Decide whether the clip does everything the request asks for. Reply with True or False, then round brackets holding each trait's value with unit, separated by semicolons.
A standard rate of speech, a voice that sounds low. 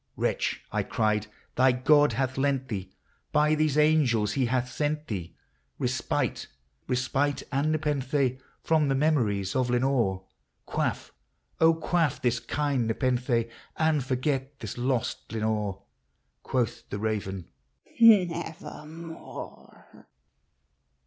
False (125 wpm; 130 Hz)